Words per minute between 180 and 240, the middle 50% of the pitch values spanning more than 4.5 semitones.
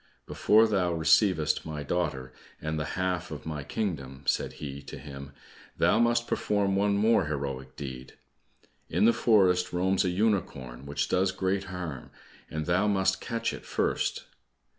No: average, 155 wpm; average, 5.2 semitones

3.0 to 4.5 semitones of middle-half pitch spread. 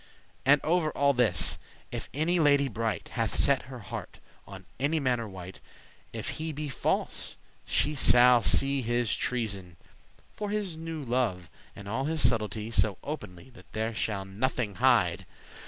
No: average, 5.2 semitones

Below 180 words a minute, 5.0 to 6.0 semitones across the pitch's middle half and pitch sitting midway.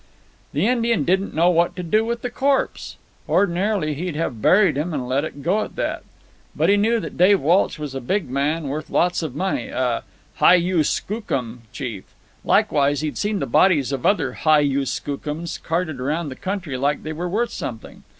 No: average, 195 wpm; average, 5.3 semitones; medium, 165 Hz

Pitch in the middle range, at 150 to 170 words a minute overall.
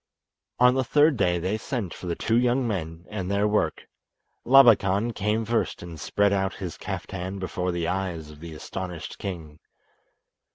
No: very low, 95 Hz; average, 165 wpm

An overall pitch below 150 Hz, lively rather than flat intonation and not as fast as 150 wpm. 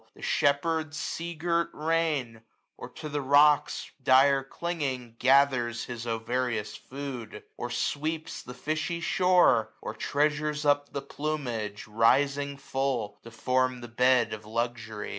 No: low, 135 Hz; average, 4.1 semitones; average, 140 wpm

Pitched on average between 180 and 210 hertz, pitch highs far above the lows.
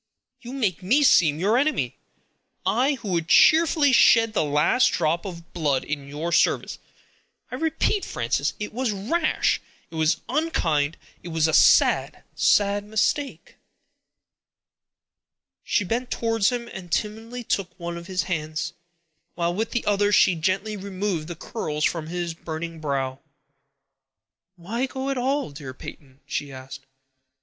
Yes: medium, 185 Hz; wide, 6.7 semitones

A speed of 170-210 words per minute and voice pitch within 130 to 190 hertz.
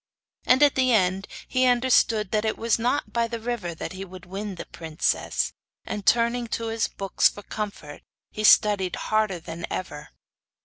No: average, 175 wpm; high, 215 Hz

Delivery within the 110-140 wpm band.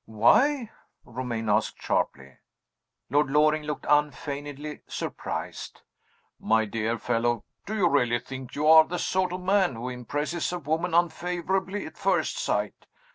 Yes: slow, 135 wpm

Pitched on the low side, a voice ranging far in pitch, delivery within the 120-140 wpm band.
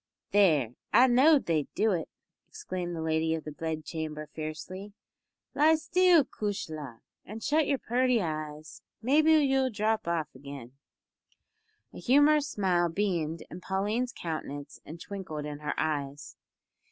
No: medium, 175 Hz; wide, 8.2 semitones; slow, 135 wpm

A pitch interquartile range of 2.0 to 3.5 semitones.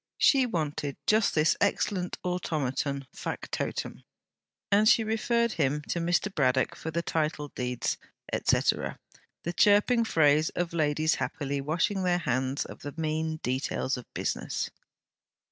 No: average, 4.7 semitones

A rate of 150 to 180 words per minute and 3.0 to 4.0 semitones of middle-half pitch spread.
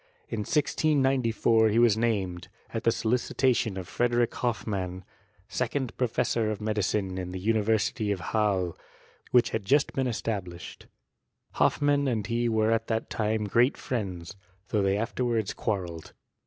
No: average, 140 wpm; average, 3.3 semitones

